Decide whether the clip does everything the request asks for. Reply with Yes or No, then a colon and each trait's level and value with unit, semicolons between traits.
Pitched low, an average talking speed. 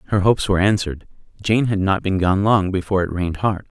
No: very low, 95 Hz; fast, 220 wpm